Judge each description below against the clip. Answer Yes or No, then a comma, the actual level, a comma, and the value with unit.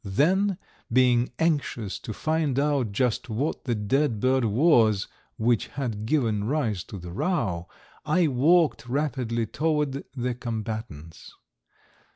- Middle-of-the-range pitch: No, low, 125 Hz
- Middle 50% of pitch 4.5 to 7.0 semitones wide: Yes, average, 5.2 semitones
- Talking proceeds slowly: Yes, slow, 125 wpm